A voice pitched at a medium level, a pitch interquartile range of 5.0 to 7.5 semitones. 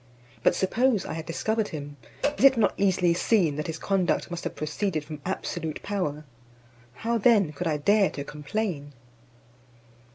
Yes: medium, 175 Hz; average, 5.3 semitones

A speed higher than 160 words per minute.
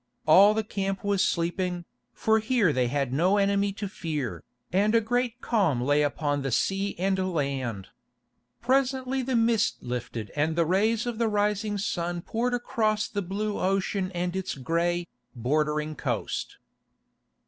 No: average, 150 wpm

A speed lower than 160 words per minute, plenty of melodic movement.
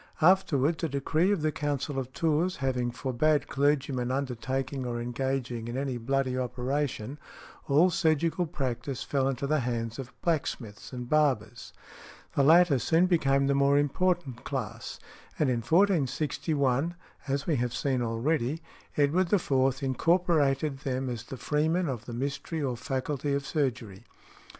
No: average, 145 wpm; average, 3.4 semitones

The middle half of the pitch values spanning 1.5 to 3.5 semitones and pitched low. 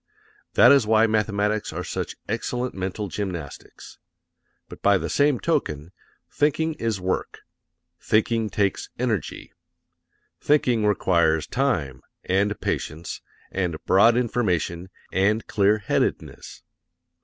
No: average, 4.0 semitones; low, 105 Hz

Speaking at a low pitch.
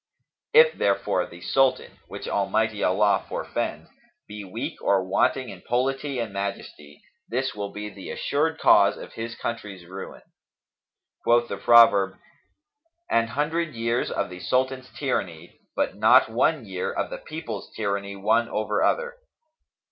Yes: low, 115 Hz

